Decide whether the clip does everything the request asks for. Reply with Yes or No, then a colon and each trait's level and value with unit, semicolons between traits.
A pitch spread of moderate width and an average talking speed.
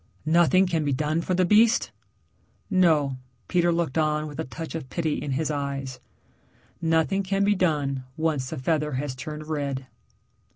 Yes: average, 3.4 semitones; average, 165 wpm